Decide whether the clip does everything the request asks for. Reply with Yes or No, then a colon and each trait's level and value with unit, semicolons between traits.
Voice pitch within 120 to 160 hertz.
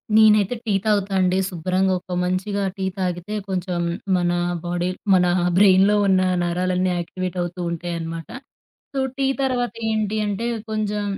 No: medium, 185 Hz